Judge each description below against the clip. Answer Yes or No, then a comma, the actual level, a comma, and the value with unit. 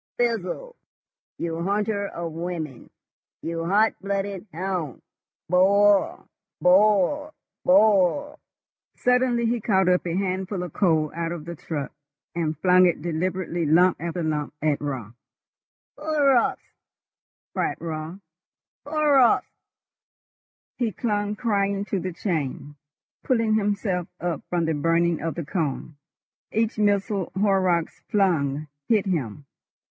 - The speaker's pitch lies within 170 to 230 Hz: Yes, medium, 185 Hz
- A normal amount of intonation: Yes, average, 4.0 semitones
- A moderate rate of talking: No, slow, 115 wpm